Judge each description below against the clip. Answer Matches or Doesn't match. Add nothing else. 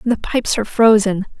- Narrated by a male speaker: Doesn't match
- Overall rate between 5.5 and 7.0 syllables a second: Matches